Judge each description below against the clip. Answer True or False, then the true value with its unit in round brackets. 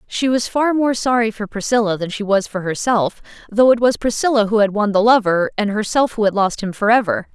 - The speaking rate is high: True (230 wpm)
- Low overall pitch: False (215 Hz)